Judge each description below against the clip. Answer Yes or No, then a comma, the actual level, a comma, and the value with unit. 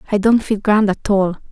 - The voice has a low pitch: No, high, 205 Hz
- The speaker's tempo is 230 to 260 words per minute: Yes, fast, 235 wpm